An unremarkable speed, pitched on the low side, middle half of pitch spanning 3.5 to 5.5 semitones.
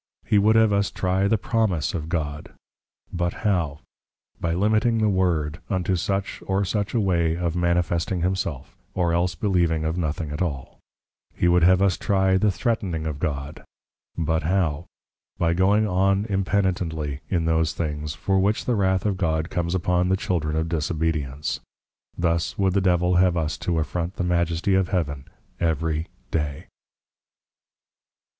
No: average, 160 wpm; very low, 90 Hz; average, 3.0 semitones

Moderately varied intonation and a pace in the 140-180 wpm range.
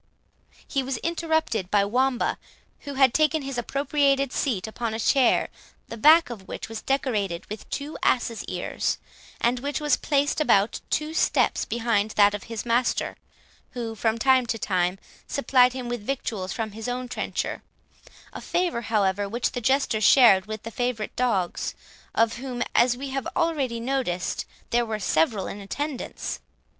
Yes: average, 3.9 semitones; average, 160 wpm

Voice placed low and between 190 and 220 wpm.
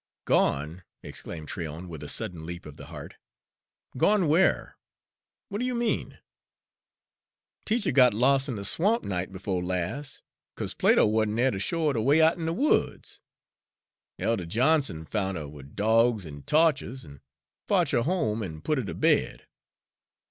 No: low, 110 Hz; average, 160 wpm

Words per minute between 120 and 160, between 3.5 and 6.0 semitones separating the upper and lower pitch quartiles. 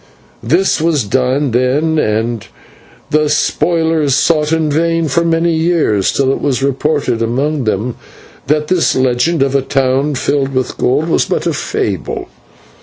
Yes: average, 150 wpm; average, 3.8 semitones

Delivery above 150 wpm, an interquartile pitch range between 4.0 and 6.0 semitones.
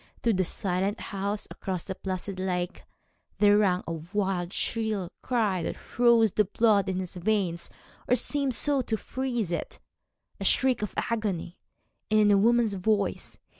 No: average, 160 wpm; average, 3.3 semitones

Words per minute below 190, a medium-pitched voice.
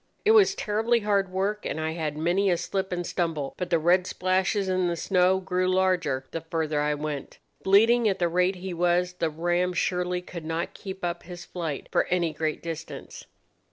No: average, 195 wpm; medium, 180 Hz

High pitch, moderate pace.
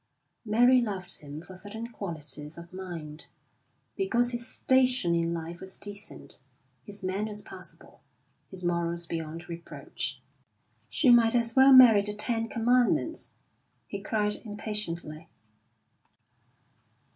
No: high, 205 Hz; slow, 115 wpm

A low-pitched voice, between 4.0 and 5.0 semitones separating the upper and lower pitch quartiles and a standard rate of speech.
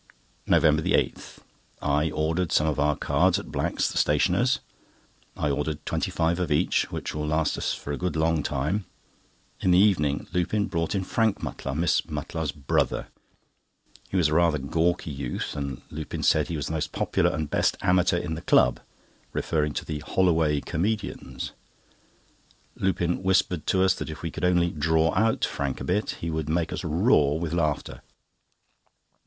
No: very low, 80 Hz; average, 3.0 semitones; average, 170 wpm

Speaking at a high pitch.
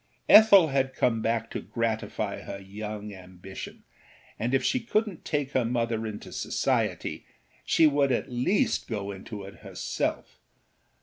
No: low, 115 Hz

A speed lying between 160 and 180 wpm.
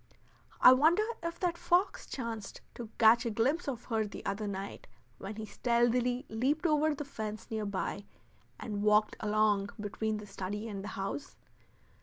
Yes: average, 165 wpm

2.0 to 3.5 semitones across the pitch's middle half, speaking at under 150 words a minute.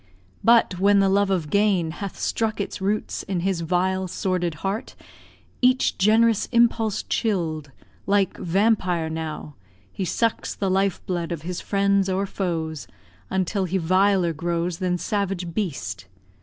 Yes: average, 2.9 semitones; average, 140 wpm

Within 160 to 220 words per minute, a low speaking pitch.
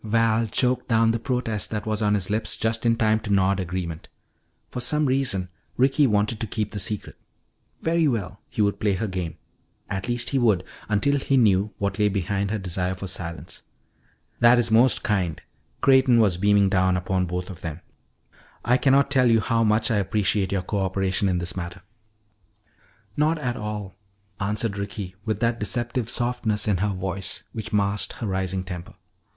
Yes: average, 180 wpm; low, 105 Hz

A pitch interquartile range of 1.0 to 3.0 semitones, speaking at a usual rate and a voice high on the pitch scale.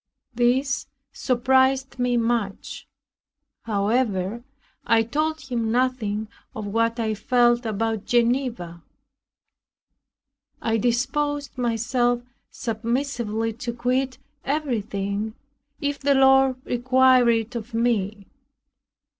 No: narrow, 2.6 semitones; slow, 90 wpm; high, 240 Hz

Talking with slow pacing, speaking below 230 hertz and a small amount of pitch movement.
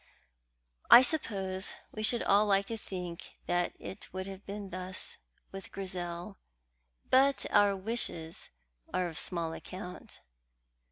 Yes: slow, 125 wpm; high, 190 Hz; narrow, 2.3 semitones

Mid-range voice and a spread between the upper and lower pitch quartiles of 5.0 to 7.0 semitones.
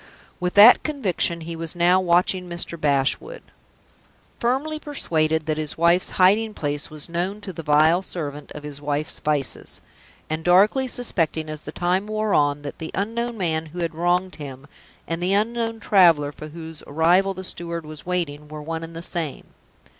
No: medium, 170 Hz; average, 3.7 semitones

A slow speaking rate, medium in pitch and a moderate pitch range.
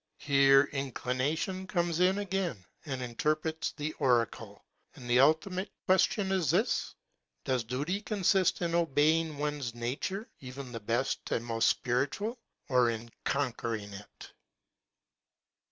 No: slow, 125 wpm; medium, 145 Hz; wide, 6.1 semitones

